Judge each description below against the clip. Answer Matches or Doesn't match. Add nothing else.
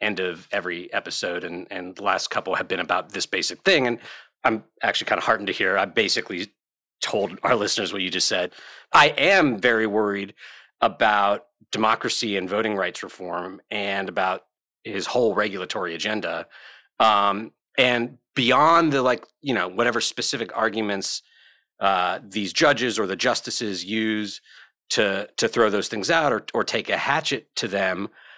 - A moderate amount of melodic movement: Matches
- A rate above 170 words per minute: Doesn't match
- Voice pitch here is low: Matches